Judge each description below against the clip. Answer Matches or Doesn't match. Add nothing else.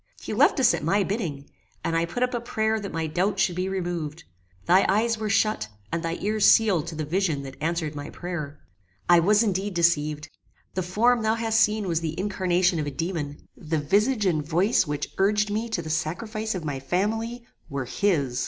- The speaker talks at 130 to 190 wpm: Doesn't match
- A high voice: Doesn't match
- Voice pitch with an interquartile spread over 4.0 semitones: Matches